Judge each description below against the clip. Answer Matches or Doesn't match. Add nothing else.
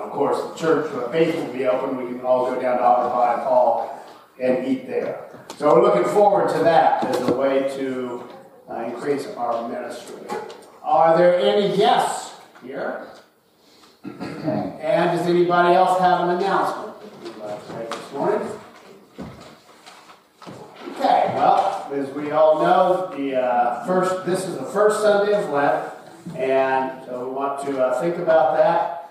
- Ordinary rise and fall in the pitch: Doesn't match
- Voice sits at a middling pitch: Matches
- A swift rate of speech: Doesn't match